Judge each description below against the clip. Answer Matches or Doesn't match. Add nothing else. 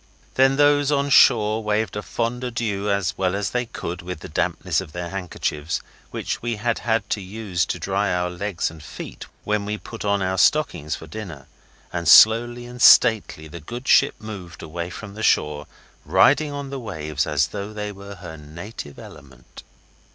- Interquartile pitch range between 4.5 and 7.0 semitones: Matches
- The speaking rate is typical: Matches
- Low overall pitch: Matches